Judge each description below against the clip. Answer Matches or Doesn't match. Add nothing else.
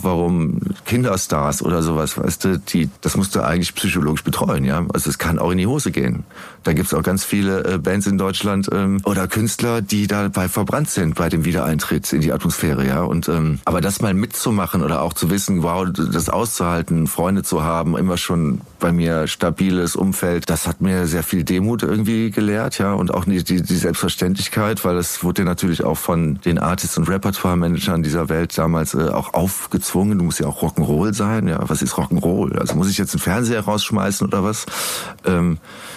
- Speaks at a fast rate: Matches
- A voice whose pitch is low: Matches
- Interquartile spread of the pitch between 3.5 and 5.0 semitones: Doesn't match